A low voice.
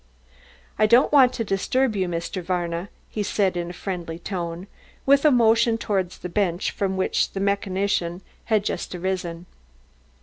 No: high, 190 Hz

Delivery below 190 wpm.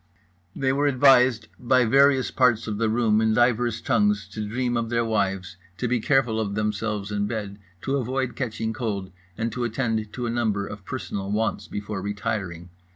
Yes: average, 180 wpm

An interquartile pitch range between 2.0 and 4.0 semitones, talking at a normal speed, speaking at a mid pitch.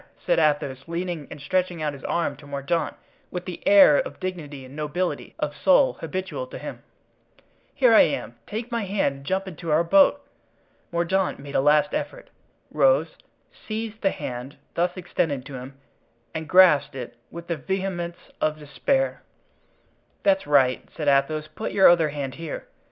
No: average, 4.8 semitones; average, 160 wpm; medium, 165 Hz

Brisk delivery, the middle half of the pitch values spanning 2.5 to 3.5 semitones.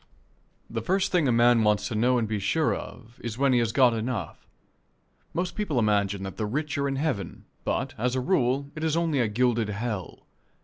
No: fast, 210 wpm; average, 4.4 semitones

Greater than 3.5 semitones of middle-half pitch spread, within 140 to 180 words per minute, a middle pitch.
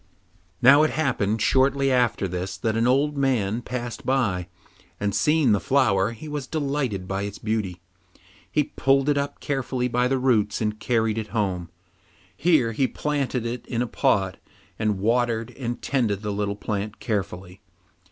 No: average, 4.7 semitones; average, 160 wpm; low, 115 Hz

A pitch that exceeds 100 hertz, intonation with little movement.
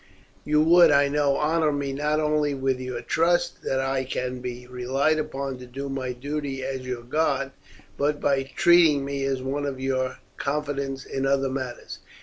Yes: low, 135 Hz; narrow, 2.2 semitones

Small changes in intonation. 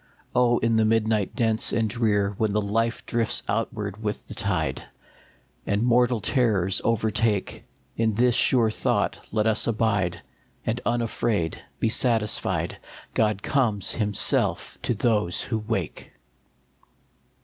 Yes: narrow, 2.0 semitones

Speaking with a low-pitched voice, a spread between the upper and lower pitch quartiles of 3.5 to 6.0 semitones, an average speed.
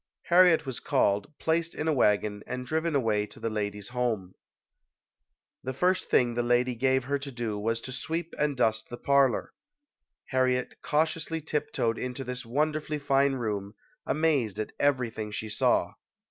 Yes: low, 125 Hz; average, 4.8 semitones; average, 160 wpm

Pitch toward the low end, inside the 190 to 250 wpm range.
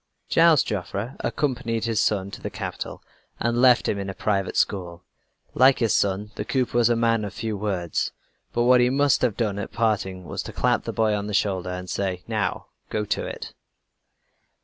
Yes: low, 105 Hz; average, 195 wpm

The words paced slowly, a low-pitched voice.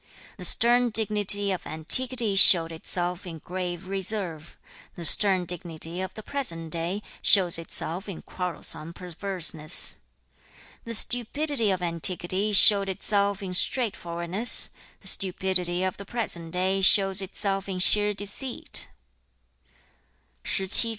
No: slow, 120 wpm; high, 190 Hz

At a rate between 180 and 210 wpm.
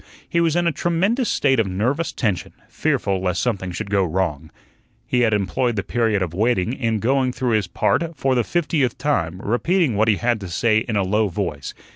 Yes: fast, 205 wpm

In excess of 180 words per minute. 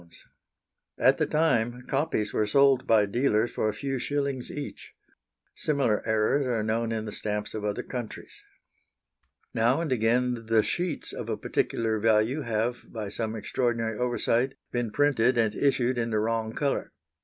No: average, 155 wpm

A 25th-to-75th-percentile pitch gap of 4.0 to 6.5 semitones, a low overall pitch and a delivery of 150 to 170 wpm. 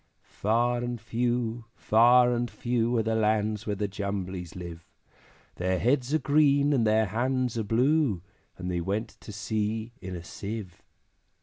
No: average, 3.3 semitones; low, 110 Hz; average, 160 wpm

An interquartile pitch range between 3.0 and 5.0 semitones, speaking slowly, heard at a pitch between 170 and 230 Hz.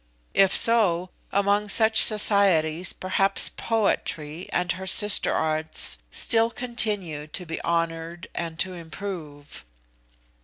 Yes: average, 4.0 semitones; slow, 110 wpm; medium, 185 Hz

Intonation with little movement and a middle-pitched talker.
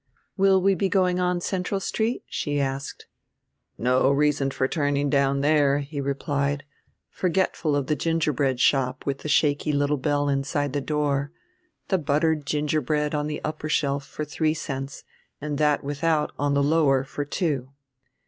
Yes: narrow, 1.9 semitones; medium, 145 Hz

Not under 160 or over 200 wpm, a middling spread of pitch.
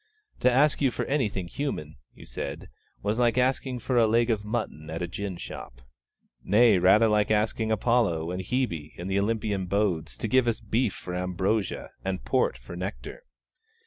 Yes: average, 175 wpm; average, 4.6 semitones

